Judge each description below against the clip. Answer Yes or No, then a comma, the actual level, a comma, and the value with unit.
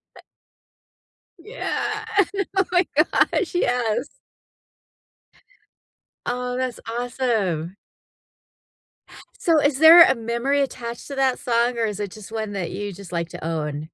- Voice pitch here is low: No, high, 240 Hz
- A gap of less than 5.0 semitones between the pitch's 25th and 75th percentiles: No, average, 5.3 semitones